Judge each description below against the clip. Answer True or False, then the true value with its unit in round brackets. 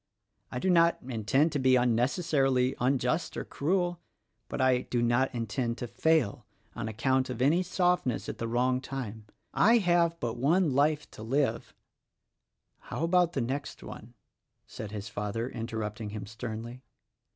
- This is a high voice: False (130 Hz)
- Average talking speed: True (160 wpm)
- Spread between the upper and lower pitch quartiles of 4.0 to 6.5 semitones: True (5.0 semitones)